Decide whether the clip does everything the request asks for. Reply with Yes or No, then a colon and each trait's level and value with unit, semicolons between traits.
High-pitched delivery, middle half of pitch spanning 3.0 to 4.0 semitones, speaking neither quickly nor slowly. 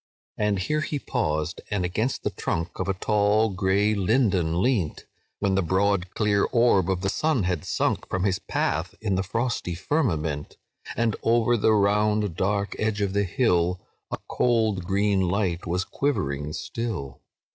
No: low, 100 Hz; average, 3.3 semitones; average, 160 wpm